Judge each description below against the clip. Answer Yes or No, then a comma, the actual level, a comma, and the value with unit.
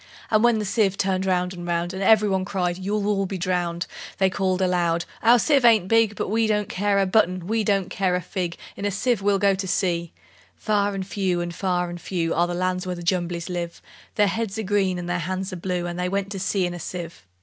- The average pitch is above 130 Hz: Yes, high, 190 Hz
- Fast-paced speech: Yes, fast, 245 wpm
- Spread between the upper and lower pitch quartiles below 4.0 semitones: Yes, narrow, 2.4 semitones